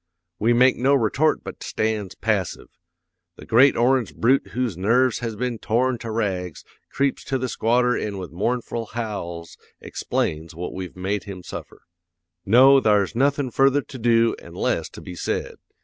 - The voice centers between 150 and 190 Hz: No, low, 115 Hz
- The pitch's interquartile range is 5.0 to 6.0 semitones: No, average, 4.3 semitones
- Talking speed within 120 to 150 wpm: No, average, 165 wpm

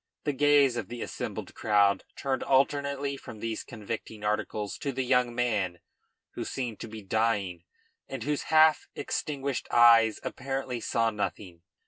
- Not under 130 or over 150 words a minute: Yes, average, 145 wpm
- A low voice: Yes, low, 120 Hz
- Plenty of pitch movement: No, average, 4.3 semitones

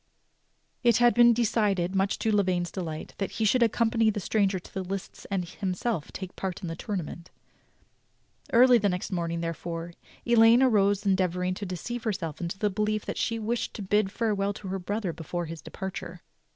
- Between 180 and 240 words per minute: Yes, average, 185 wpm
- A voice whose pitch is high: Yes, high, 195 Hz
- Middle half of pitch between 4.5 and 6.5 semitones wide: No, average, 3.5 semitones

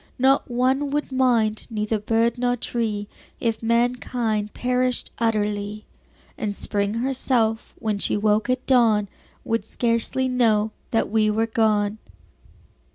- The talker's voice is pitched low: No, high, 225 Hz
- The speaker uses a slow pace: Yes, slow, 125 wpm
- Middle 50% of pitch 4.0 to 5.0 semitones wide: No, average, 2.7 semitones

